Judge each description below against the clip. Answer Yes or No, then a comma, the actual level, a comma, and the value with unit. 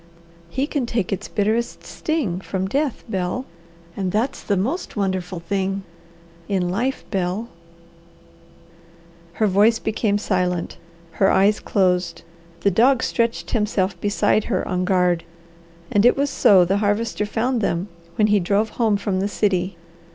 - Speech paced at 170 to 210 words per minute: No, average, 145 wpm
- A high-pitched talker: Yes, high, 200 Hz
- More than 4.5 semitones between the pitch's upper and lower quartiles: No, average, 3.6 semitones